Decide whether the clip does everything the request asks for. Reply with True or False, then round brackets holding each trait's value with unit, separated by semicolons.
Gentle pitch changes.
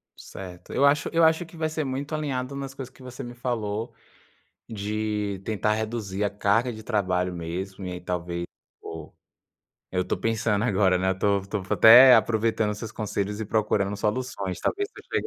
False (4.3 semitones)